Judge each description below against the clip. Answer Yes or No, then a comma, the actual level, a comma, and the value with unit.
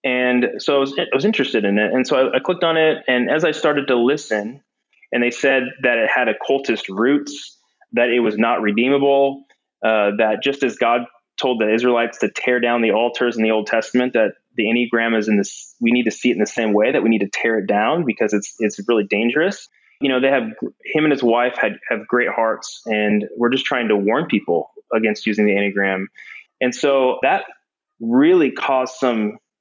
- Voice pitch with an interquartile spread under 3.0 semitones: No, average, 3.8 semitones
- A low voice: Yes, low, 120 Hz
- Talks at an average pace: No, fast, 215 wpm